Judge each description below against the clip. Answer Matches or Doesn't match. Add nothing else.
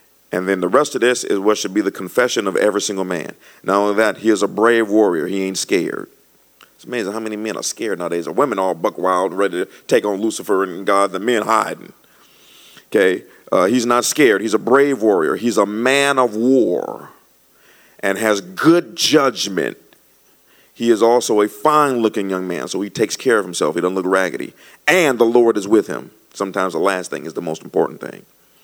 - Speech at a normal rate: Doesn't match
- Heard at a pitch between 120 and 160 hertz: Doesn't match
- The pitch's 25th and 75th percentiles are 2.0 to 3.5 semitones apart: Doesn't match